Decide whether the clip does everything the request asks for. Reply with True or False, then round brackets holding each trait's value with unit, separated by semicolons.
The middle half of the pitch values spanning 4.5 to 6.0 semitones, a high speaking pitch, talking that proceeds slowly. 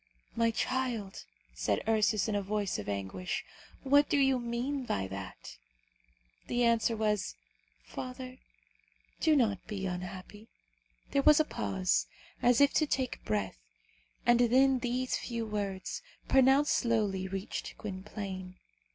True (5.2 semitones; 220 Hz; 130 wpm)